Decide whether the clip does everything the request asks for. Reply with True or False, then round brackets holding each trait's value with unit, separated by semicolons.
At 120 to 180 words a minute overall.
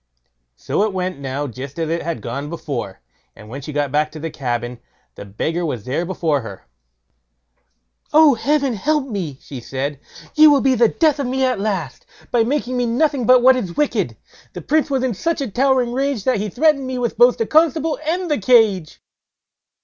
False (195 wpm)